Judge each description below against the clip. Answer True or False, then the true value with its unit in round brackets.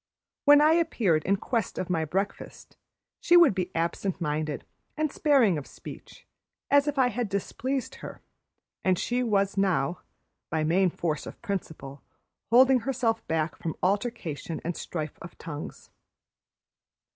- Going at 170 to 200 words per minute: False (145 wpm)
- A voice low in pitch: False (195 Hz)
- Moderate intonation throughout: False (7.3 semitones)